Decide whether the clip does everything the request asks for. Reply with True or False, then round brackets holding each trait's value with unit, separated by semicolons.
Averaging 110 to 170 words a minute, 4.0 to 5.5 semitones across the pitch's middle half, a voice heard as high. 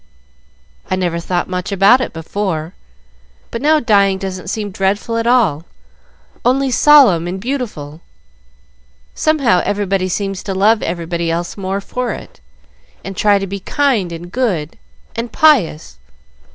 True (140 wpm; 4.8 semitones; 195 Hz)